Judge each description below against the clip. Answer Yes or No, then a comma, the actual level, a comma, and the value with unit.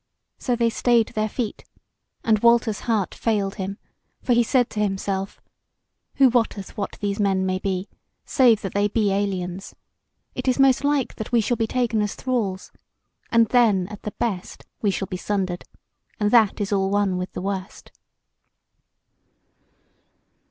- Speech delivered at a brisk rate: No, average, 160 wpm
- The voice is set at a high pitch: Yes, high, 210 Hz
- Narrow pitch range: No, average, 3.3 semitones